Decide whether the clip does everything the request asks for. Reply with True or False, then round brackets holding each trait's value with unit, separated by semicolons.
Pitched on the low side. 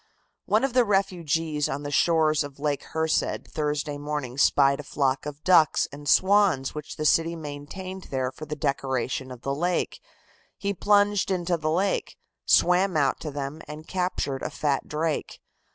False (155 Hz)